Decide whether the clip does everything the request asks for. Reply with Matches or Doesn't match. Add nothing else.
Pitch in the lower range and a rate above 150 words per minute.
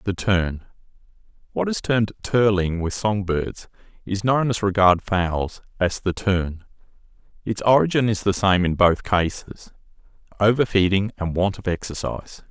Doesn't match